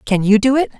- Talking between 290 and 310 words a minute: Yes, fast, 300 wpm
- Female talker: Yes, female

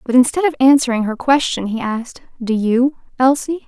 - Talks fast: No, average, 180 wpm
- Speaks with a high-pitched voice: Yes, very high, 255 Hz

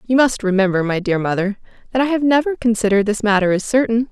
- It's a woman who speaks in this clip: Yes, female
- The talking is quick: Yes, fast, 220 wpm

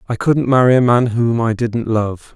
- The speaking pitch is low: Yes, low, 120 Hz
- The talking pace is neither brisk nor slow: No, fast, 230 wpm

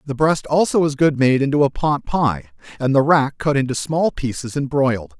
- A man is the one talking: Yes, male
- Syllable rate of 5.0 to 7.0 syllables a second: Yes, 5.1 syllables/s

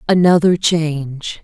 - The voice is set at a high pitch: No, medium, 165 Hz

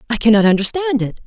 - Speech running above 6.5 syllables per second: Yes, 6.9 syllables/s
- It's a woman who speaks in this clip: Yes, female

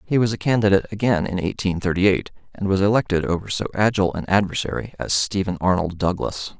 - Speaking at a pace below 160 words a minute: No, average, 190 wpm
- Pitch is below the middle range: Yes, very low, 95 Hz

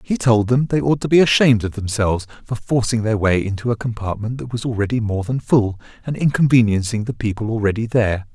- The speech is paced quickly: Yes, fast, 210 wpm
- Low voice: Yes, low, 115 Hz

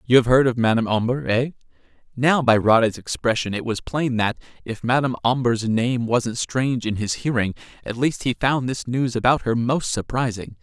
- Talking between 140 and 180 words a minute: No, average, 190 wpm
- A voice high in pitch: No, low, 120 Hz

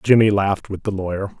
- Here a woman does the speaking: No, male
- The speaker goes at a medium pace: No, fast, 215 wpm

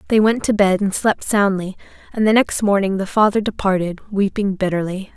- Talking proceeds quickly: No, average, 185 wpm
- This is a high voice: Yes, high, 200 Hz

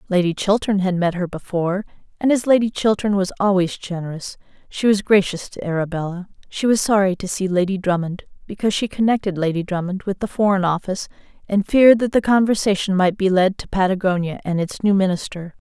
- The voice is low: No, high, 190 Hz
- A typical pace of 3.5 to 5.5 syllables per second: No, 6.0 syllables/s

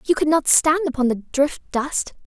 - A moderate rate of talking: No, fast, 210 wpm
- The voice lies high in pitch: Yes, very high, 290 Hz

